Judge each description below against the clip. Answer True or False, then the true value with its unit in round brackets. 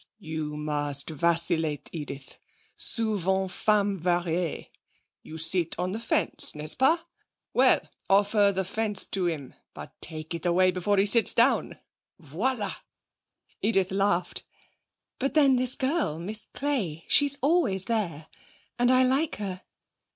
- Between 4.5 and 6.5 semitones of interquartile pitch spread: True (5.4 semitones)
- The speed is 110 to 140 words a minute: True (135 wpm)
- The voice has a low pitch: False (190 Hz)